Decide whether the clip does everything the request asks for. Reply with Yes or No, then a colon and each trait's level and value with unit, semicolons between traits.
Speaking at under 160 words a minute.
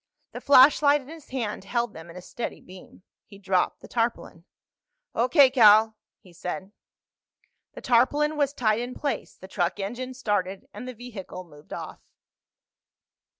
Yes: average, 150 wpm